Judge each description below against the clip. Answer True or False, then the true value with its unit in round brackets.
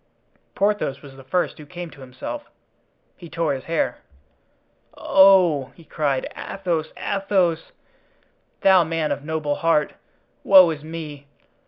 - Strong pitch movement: False (3.8 semitones)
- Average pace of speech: False (130 wpm)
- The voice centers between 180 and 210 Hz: False (160 Hz)